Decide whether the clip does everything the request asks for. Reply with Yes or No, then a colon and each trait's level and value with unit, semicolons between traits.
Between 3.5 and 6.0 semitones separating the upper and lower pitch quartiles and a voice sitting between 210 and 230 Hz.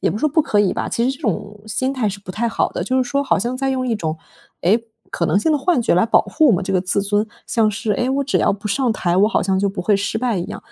Yes: average, 4.4 semitones; high, 220 Hz